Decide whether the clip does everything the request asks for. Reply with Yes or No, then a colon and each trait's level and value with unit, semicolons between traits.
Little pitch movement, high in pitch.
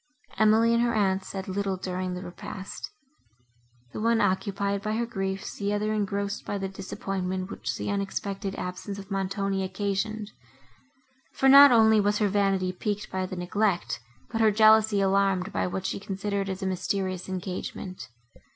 Yes: narrow, 1.8 semitones; high, 195 Hz